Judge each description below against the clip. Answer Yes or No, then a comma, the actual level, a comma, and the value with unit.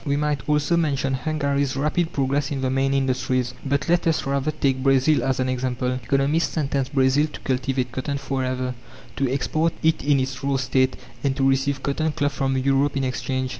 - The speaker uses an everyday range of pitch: No, narrow, 1.7 semitones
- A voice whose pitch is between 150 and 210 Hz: No, low, 135 Hz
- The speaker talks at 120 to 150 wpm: No, average, 190 wpm